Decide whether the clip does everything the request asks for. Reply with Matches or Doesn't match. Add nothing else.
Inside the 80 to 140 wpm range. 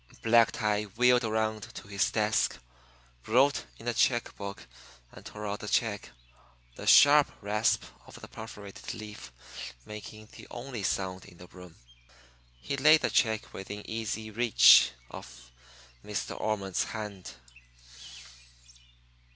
Matches